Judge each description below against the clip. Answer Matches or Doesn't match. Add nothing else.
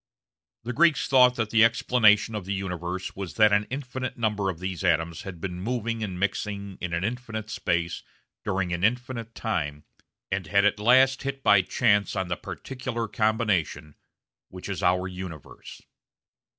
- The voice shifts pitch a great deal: Doesn't match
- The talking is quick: Doesn't match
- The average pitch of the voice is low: Matches